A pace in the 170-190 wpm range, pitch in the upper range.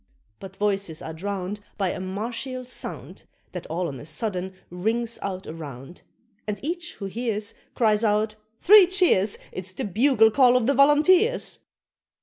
No: average, 150 wpm; high, 210 Hz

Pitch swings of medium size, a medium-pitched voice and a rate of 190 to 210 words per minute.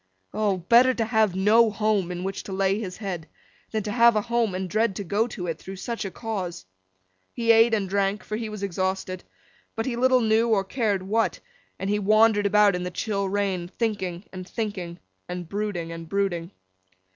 No: average, 3.0 semitones; high, 200 Hz; average, 195 wpm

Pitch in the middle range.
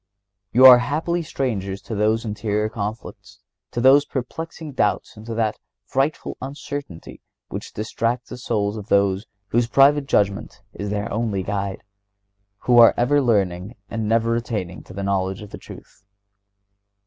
No: low, 115 Hz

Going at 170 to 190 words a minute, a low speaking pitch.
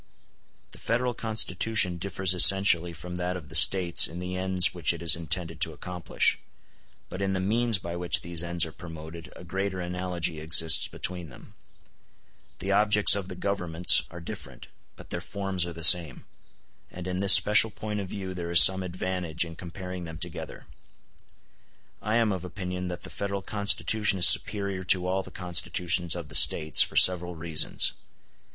Yes: average, 175 wpm; very low, 90 Hz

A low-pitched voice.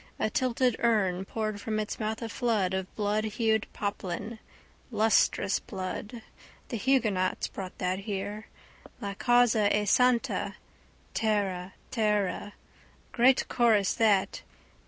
No: high, 215 Hz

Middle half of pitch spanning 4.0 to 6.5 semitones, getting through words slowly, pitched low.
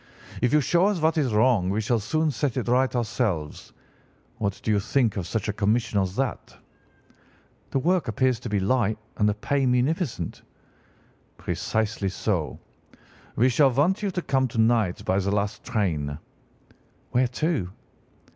No: average, 4.7 semitones; average, 165 wpm; low, 115 Hz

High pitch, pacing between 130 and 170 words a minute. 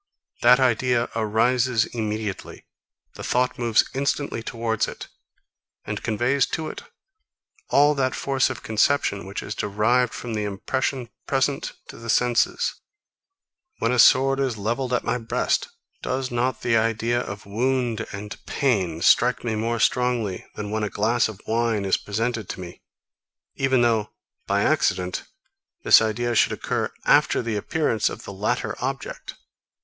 No: low, 115 Hz; average, 150 wpm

